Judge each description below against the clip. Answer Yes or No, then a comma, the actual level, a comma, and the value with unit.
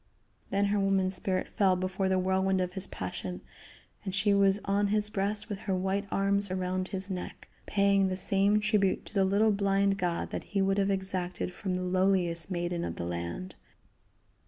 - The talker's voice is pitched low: No, high, 190 Hz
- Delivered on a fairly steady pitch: Yes, narrow, 1.4 semitones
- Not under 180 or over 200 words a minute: Yes, average, 185 wpm